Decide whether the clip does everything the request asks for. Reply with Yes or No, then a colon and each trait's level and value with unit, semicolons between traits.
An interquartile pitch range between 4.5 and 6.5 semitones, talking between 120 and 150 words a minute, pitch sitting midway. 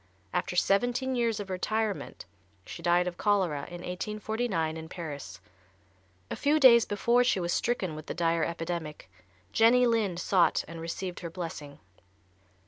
Yes: average, 5.0 semitones; average, 145 wpm; medium, 180 Hz